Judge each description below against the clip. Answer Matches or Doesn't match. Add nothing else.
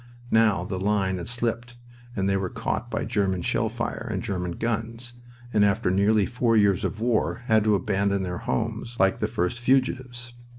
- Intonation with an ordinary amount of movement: Matches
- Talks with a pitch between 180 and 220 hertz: Doesn't match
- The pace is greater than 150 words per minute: Matches